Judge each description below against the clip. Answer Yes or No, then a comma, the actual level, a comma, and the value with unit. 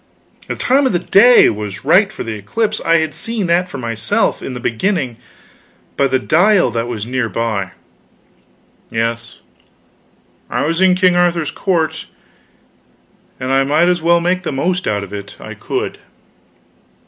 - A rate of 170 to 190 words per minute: No, average, 160 wpm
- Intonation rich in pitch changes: Yes, wide, 7.8 semitones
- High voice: No, medium, 155 Hz